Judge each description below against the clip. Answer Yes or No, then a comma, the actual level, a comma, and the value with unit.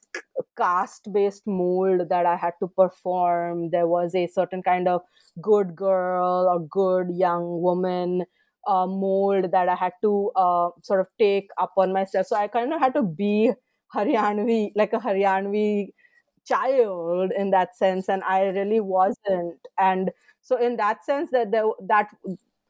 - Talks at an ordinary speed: Yes, average, 155 wpm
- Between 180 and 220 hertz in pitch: Yes, high, 190 Hz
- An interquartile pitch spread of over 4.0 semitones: No, average, 2.7 semitones